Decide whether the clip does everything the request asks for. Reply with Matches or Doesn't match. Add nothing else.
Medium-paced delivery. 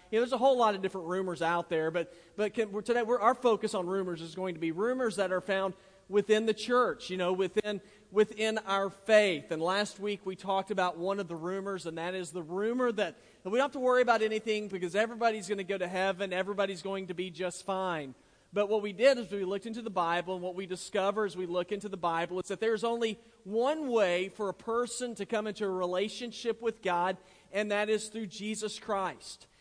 Doesn't match